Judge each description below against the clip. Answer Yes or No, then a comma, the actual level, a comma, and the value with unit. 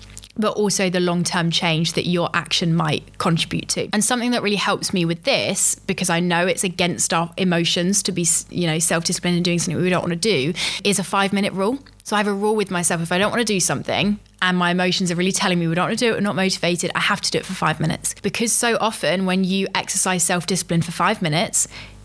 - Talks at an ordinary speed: No, fast, 250 wpm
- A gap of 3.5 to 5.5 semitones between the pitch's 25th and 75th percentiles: No, average, 2.8 semitones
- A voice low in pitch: No, medium, 180 Hz